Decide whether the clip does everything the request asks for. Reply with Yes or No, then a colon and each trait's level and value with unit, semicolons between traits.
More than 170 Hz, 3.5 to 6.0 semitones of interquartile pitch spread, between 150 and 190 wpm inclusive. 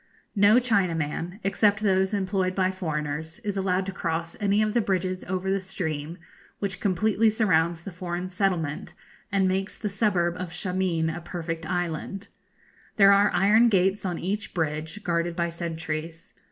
No: medium, 185 Hz; average, 2.9 semitones; average, 155 wpm